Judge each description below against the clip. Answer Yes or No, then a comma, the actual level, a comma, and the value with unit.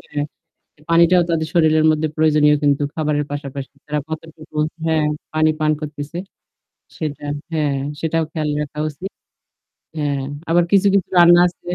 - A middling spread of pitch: No, narrow, 1.7 semitones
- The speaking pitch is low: No, medium, 155 Hz